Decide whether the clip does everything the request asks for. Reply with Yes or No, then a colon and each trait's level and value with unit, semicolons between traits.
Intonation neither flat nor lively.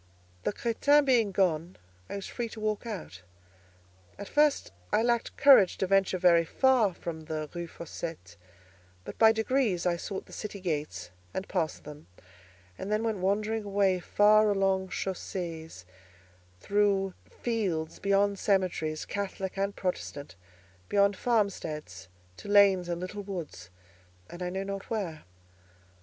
Yes: average, 3.5 semitones